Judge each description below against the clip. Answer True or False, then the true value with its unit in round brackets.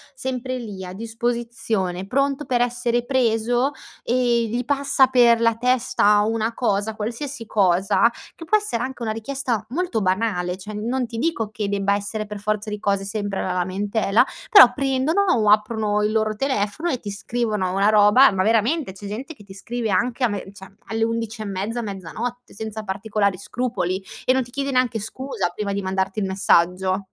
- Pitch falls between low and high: False (220 Hz)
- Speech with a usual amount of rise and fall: True (3.5 semitones)